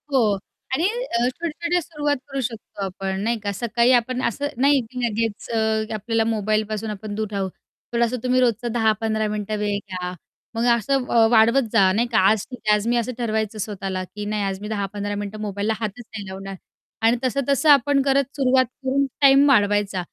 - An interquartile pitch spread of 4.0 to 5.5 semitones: No, average, 3.6 semitones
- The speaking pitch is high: Yes, high, 225 Hz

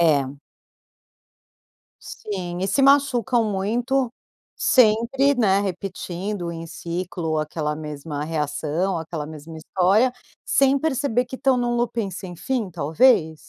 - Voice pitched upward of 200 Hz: No, high, 190 Hz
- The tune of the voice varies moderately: No, wide, 7.1 semitones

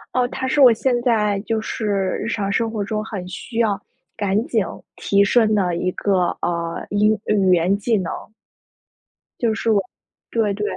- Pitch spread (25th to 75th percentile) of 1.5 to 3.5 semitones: Yes, narrow, 2.5 semitones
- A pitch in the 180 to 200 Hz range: No, high, 210 Hz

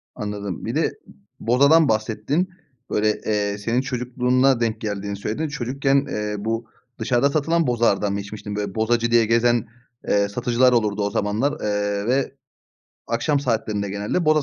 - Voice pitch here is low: Yes, low, 115 Hz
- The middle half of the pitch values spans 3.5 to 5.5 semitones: Yes, average, 3.8 semitones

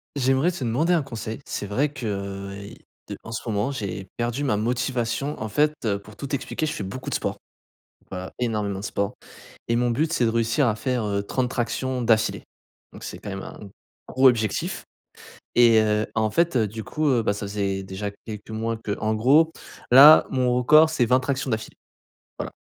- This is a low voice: Yes, low, 115 Hz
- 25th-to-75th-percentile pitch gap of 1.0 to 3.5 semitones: No, average, 3.9 semitones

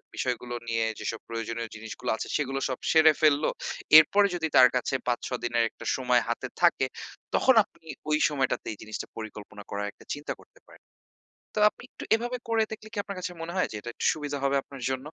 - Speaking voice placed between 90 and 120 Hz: No, low, 135 Hz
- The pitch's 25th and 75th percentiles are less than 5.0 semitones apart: No, wide, 5.6 semitones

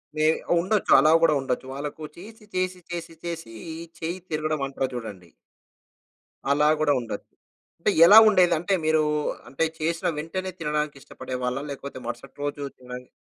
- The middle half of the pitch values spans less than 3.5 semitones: No, average, 4.0 semitones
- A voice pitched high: No, medium, 155 Hz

